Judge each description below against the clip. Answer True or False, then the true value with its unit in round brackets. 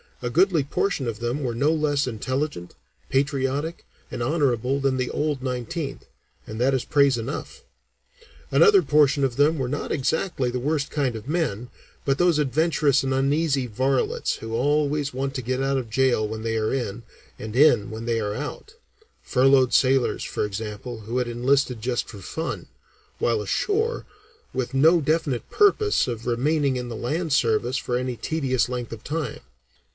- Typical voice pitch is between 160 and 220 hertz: False (130 Hz)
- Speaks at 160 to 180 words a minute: True (170 wpm)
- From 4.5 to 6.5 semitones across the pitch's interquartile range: False (3.6 semitones)